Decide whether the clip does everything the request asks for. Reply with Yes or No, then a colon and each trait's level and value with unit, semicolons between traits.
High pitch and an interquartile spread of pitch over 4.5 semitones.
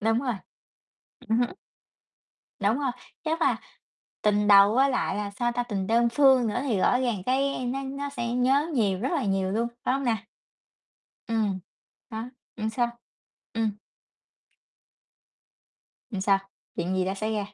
No: high, 230 Hz; average, 4.0 semitones